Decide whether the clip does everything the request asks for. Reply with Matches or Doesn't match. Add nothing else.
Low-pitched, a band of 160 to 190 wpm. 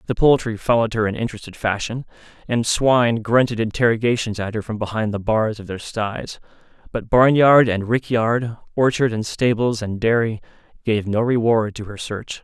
Matches